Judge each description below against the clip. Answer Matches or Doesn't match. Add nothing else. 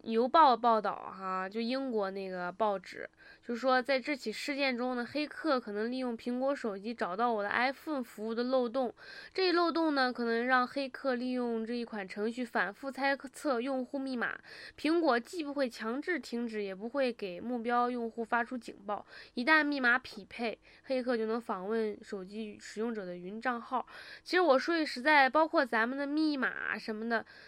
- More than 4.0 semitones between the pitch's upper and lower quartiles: Doesn't match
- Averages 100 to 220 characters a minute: Doesn't match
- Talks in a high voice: Matches